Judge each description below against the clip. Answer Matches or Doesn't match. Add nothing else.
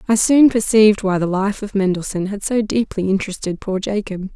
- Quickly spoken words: Doesn't match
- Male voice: Doesn't match